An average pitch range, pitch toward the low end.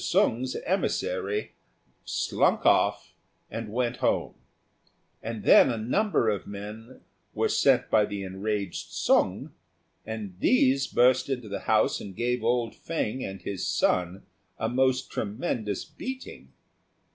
Yes: average, 3.9 semitones; low, 115 Hz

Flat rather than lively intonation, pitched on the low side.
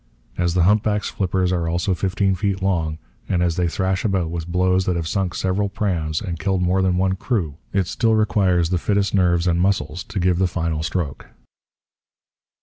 Yes: narrow, 2.1 semitones; very low, 90 Hz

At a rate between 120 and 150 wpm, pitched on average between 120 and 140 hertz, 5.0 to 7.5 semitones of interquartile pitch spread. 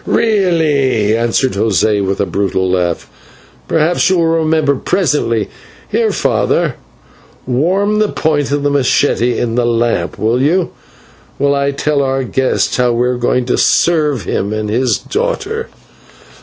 Yes: average, 145 wpm; low, 135 Hz; wide, 5.6 semitones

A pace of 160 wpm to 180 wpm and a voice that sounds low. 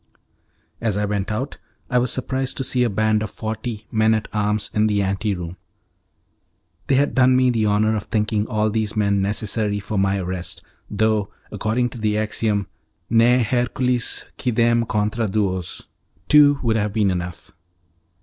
Yes: average, 165 wpm; low, 110 Hz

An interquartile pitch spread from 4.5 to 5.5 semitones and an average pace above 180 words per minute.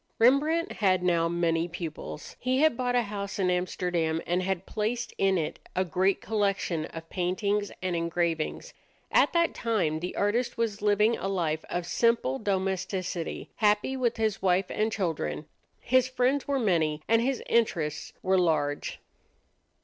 No: average, 4.9 semitones; average, 155 wpm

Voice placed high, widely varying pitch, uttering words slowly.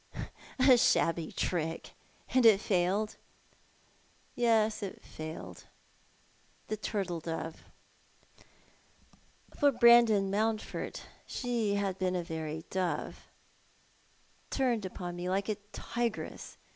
No: high, 200 Hz; average, 4.4 semitones; slow, 120 wpm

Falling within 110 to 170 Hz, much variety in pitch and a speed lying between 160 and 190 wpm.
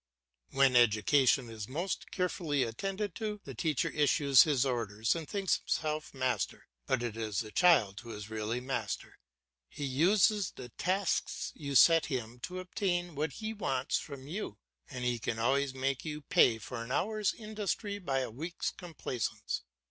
Yes: medium, 140 Hz; wide, 6.6 semitones; average, 165 wpm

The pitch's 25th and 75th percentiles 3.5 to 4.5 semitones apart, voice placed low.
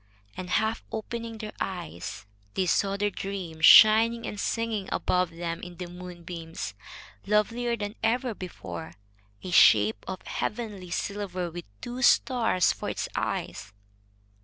No: average, 4.2 semitones; high, 195 Hz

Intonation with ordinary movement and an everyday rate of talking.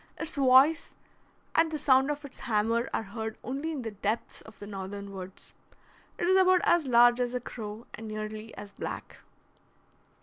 Yes: average, 5.0 semitones; average, 175 wpm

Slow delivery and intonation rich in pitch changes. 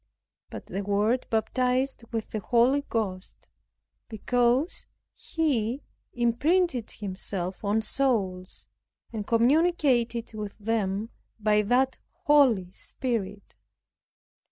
No: slow, 90 wpm; average, 3.8 semitones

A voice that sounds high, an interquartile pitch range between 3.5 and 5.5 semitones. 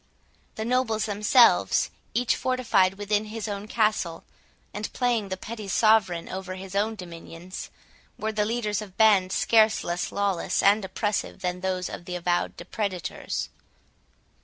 No: high, 205 Hz; average, 2.8 semitones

